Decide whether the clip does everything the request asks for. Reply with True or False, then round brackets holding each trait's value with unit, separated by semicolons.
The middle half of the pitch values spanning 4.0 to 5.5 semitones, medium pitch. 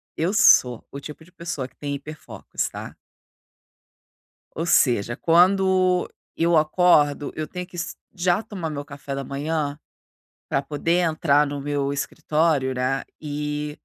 False (3.3 semitones; 150 Hz)